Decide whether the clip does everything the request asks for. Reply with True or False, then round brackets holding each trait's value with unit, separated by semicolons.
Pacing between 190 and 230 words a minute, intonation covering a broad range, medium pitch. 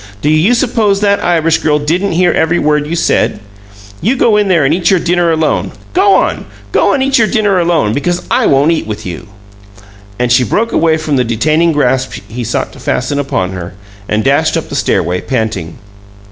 True (200 wpm; 6.3 semitones; 155 Hz)